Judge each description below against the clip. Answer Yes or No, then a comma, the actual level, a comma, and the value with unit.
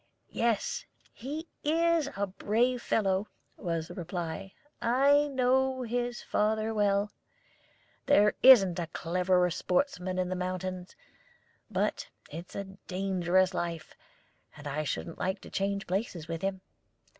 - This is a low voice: No, high, 195 Hz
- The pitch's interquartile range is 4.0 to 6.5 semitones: Yes, average, 5.0 semitones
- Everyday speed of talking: No, slow, 125 wpm